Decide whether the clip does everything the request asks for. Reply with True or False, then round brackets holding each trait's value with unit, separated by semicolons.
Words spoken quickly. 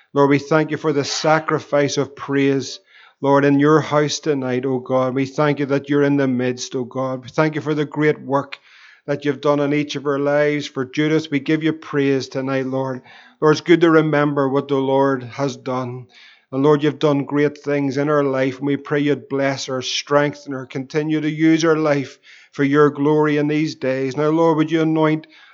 True (220 wpm)